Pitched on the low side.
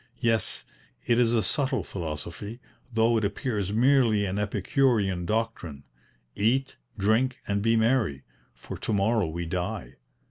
Yes: low, 110 Hz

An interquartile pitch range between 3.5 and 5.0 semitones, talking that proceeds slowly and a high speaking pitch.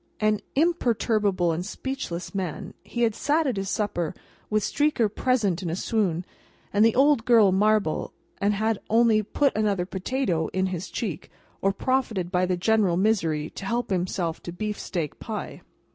No: average, 4.1 semitones; average, 160 wpm; high, 205 Hz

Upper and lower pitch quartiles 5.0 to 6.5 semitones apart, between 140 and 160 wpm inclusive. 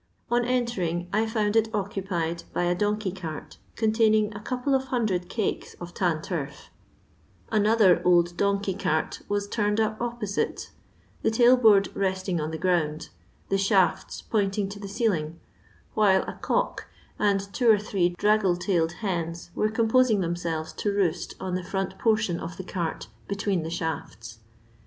No: average, 3.6 semitones; average, 155 wpm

